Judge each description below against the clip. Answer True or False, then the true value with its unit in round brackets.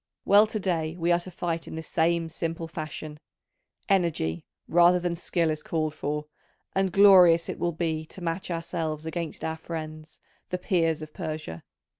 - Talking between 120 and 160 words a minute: False (170 wpm)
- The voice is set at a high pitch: False (165 Hz)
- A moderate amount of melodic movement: False (1.9 semitones)